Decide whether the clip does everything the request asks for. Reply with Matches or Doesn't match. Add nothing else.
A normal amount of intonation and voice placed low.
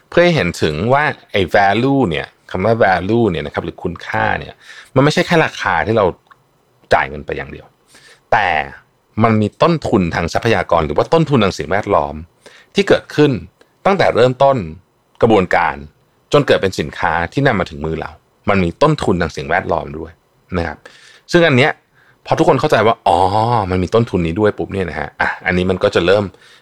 Doesn't match